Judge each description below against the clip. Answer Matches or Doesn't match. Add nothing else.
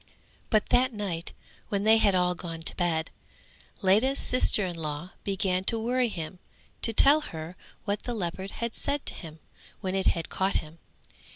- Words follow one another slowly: Doesn't match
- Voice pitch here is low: Doesn't match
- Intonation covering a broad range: Doesn't match